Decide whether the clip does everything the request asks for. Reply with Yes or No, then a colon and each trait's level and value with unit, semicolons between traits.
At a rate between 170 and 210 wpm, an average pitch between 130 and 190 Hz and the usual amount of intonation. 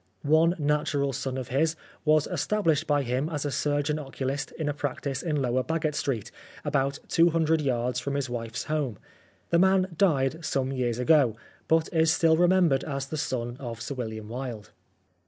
Yes: average, 175 wpm; medium, 140 Hz; average, 3.6 semitones